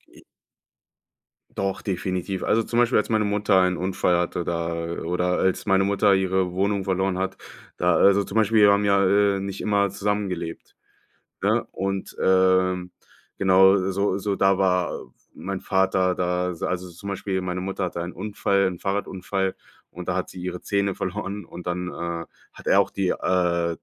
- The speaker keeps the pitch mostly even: Yes, narrow, 1.6 semitones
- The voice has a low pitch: Yes, very low, 95 Hz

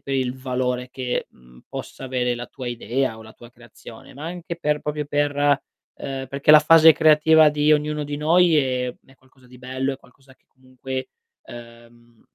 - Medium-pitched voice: No, low, 130 Hz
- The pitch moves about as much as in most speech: Yes, average, 3.1 semitones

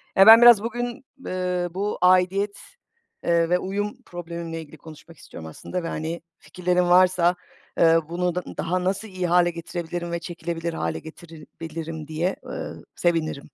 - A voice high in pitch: No, medium, 175 Hz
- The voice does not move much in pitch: Yes, narrow, 1.9 semitones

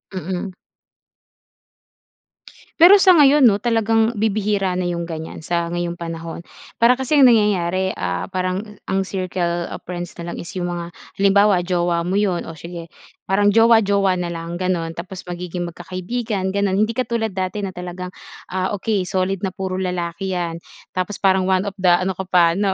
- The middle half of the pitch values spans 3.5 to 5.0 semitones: No, narrow, 2.6 semitones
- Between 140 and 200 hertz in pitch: Yes, medium, 185 Hz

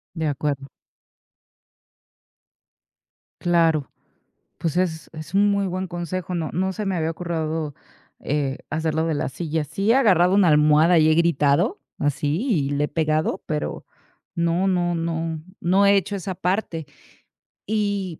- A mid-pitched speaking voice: Yes, medium, 165 Hz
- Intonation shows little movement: No, average, 3.1 semitones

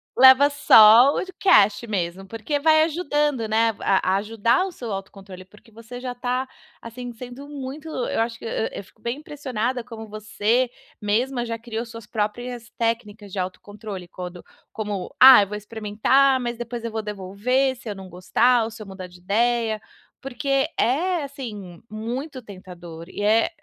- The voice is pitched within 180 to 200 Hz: No, high, 230 Hz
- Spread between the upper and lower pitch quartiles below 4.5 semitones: Yes, average, 3.6 semitones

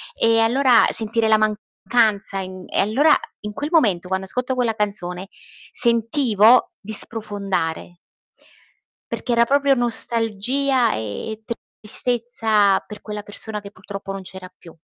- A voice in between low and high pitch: No, high, 215 Hz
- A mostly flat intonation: No, average, 3.2 semitones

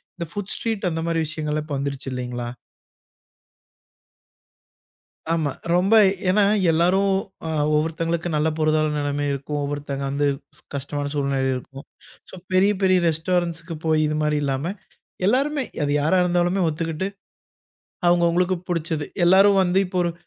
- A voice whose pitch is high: No, medium, 160 Hz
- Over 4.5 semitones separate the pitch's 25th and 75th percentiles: No, average, 3.7 semitones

